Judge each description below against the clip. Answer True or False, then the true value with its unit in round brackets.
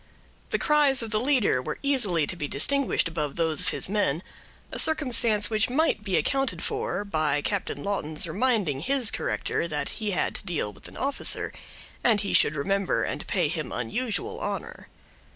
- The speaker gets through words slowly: False (175 wpm)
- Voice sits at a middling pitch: False (205 Hz)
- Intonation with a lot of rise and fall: True (8.2 semitones)